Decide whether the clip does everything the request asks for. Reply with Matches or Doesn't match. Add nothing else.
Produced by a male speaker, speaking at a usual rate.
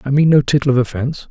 Doesn't match